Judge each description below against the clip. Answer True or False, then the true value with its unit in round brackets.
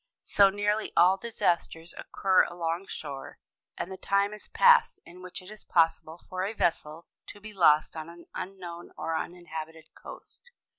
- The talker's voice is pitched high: False (180 Hz)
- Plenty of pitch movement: False (3.3 semitones)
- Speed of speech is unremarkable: True (160 wpm)